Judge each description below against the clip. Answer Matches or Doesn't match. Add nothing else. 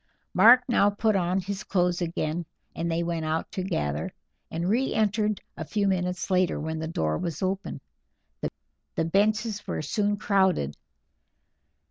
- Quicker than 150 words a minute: Doesn't match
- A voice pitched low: Doesn't match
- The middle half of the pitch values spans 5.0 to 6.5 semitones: Doesn't match